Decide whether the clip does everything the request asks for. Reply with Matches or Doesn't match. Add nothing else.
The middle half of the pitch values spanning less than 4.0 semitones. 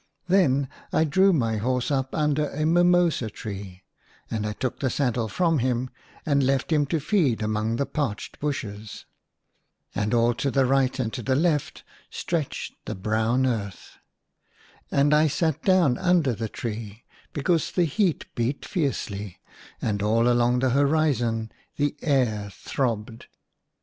Doesn't match